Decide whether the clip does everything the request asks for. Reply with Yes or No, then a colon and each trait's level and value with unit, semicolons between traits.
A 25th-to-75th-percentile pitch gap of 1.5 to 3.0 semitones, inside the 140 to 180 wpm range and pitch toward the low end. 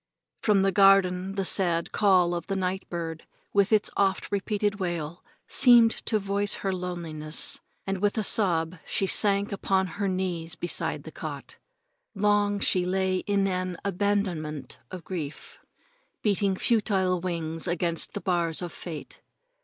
No: narrow, 2.6 semitones; average, 145 wpm; high, 190 Hz